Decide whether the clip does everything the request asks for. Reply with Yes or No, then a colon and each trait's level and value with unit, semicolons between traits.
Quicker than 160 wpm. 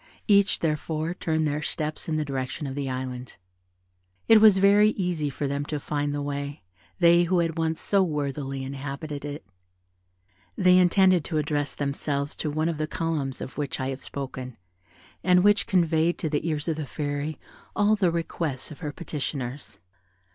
Yes: average, 175 wpm